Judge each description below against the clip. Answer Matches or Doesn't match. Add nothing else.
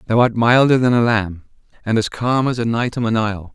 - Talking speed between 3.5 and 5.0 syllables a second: Doesn't match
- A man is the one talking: Matches